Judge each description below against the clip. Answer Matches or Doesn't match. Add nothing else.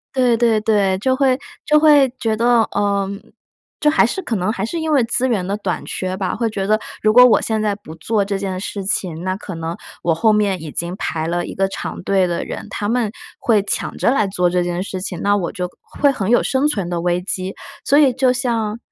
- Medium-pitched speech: Doesn't match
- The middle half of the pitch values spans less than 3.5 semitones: Doesn't match